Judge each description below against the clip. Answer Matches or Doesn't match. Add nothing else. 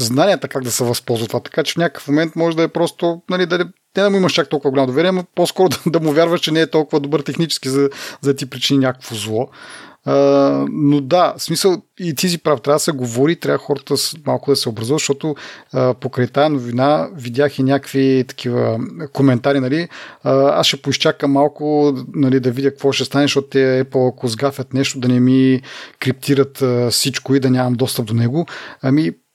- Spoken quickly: Matches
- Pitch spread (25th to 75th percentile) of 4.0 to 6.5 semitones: Doesn't match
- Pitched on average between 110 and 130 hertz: Doesn't match